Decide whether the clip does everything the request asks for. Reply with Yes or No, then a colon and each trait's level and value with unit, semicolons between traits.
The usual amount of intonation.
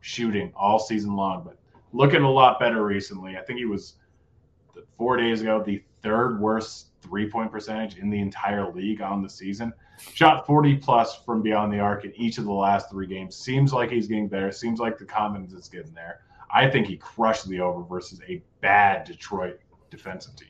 Yes: average, 3.0 semitones